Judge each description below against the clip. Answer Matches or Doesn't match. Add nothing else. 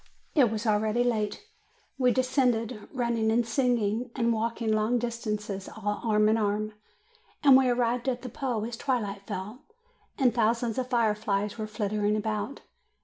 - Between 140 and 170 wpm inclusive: Matches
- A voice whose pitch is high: Matches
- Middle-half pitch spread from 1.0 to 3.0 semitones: Matches